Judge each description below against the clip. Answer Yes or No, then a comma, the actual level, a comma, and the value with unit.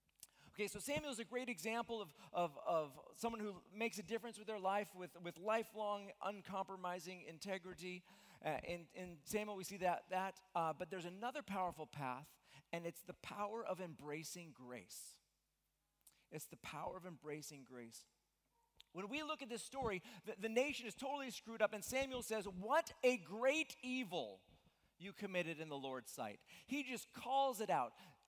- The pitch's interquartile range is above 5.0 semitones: Yes, wide, 5.5 semitones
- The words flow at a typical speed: Yes, average, 170 wpm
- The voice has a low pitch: No, high, 190 Hz